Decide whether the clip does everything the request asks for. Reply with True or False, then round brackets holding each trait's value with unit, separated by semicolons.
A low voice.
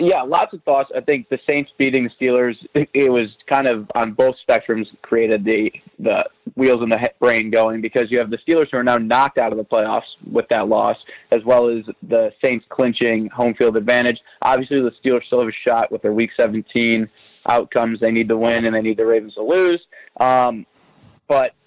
True (120 Hz)